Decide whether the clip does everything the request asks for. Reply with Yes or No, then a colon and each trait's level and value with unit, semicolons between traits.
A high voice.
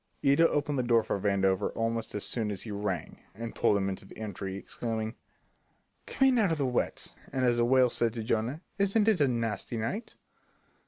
No: low, 115 Hz